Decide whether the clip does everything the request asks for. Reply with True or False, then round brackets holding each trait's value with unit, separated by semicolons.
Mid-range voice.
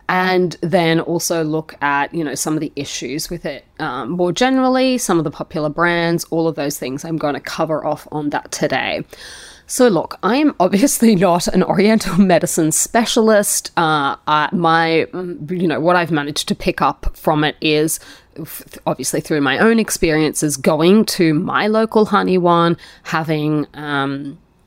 True (170 Hz)